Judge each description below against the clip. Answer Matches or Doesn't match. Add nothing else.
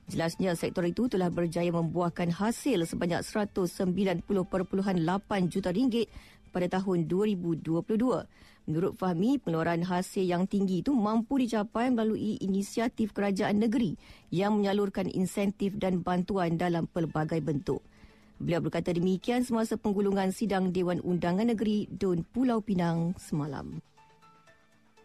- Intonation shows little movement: Doesn't match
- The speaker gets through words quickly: Doesn't match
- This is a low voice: Doesn't match